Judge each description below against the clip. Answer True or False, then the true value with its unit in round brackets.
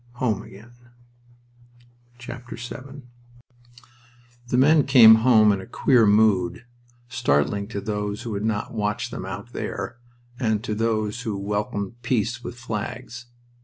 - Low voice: True (110 Hz)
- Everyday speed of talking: False (130 wpm)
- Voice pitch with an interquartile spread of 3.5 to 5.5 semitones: False (2.8 semitones)